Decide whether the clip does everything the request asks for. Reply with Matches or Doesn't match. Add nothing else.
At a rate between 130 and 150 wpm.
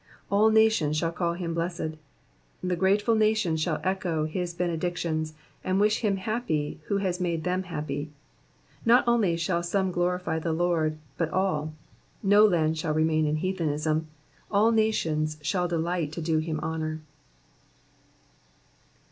Matches